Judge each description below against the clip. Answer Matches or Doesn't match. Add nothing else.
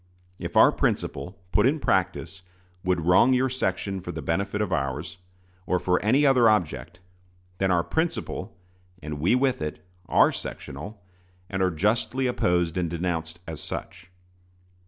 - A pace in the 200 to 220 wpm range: Doesn't match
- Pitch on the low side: Matches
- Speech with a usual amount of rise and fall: Matches